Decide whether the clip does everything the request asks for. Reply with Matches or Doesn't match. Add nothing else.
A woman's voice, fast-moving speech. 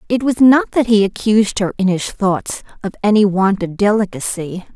Doesn't match